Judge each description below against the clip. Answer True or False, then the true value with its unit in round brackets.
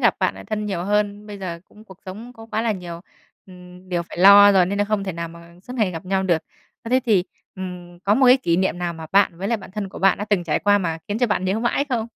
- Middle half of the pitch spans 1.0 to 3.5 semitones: True (2.9 semitones)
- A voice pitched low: False (195 Hz)